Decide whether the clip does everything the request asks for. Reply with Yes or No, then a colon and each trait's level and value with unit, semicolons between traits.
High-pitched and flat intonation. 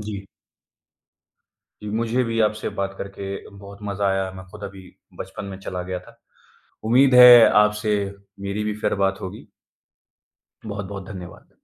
No: low, 100 Hz; narrow, 1.8 semitones